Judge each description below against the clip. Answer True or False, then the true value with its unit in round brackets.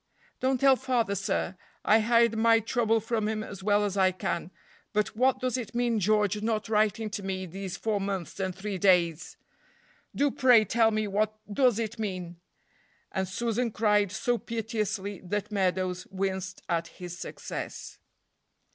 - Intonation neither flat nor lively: True (3.1 semitones)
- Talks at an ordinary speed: True (160 wpm)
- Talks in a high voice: True (210 Hz)